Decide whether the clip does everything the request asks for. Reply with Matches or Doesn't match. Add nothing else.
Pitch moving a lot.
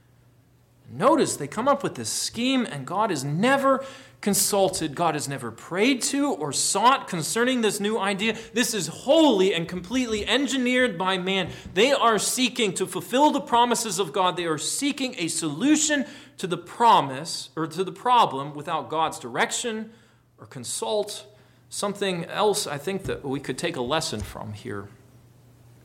Matches